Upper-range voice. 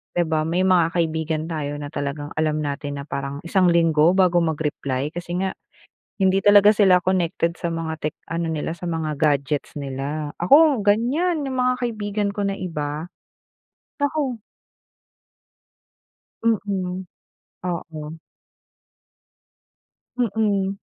No: medium, 170 Hz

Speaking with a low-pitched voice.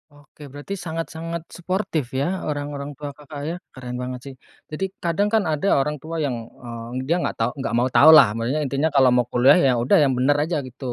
No: medium, 145 Hz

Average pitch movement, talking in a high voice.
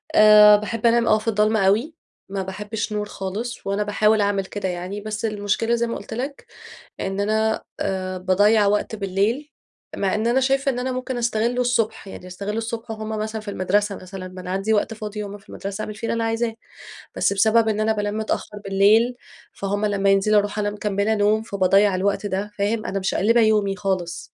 No: narrow, 2.0 semitones; high, 210 Hz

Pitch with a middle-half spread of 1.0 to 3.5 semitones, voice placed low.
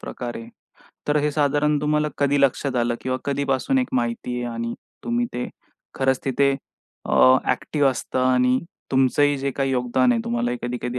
Yes: narrow, 2.6 semitones; low, 130 Hz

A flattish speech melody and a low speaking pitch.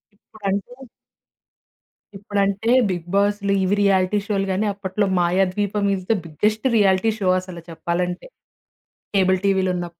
No: narrow, 1.8 semitones; high, 195 Hz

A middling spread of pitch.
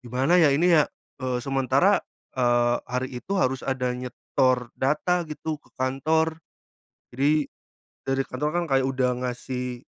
Yes: average, 3.1 semitones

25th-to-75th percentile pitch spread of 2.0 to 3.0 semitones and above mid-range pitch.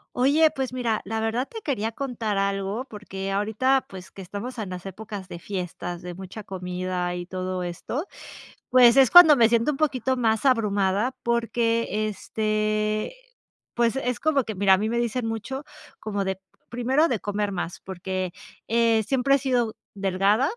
No: average, 4.3 semitones; high, 220 Hz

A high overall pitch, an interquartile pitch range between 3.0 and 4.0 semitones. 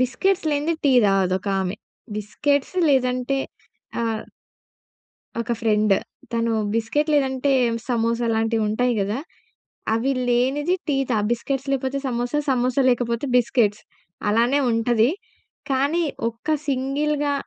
Yes: high, 245 Hz; average, 3.4 semitones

